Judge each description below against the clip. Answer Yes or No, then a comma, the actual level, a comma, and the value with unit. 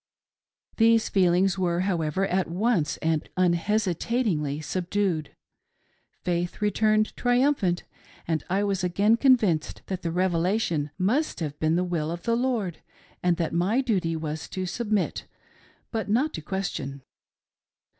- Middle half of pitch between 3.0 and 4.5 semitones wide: Yes, average, 4.2 semitones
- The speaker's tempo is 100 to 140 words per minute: Yes, slow, 135 wpm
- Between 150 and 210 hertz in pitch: Yes, medium, 185 Hz